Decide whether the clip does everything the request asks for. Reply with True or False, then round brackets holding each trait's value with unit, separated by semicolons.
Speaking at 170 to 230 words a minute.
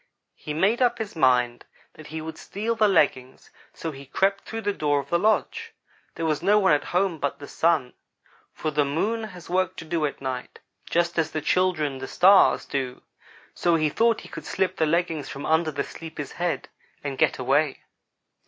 True (200 wpm)